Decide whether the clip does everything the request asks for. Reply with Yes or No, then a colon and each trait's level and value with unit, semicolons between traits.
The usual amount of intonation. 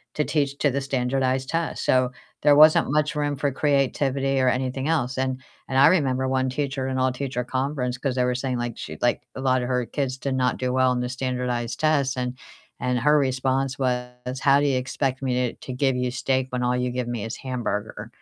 No: narrow, 1.5 semitones